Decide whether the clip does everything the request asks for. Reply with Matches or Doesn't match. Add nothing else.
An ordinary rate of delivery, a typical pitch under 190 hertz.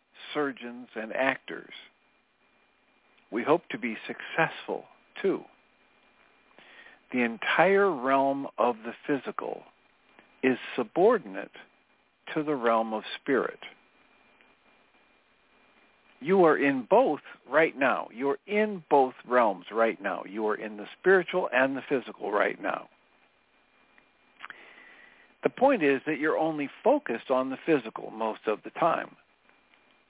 Doesn't match